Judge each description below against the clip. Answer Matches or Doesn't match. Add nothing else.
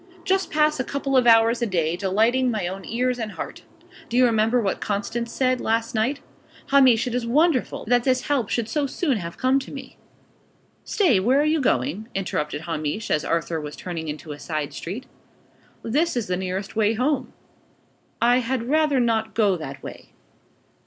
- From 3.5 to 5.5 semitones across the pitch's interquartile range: Matches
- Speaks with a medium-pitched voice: Doesn't match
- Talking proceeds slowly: Doesn't match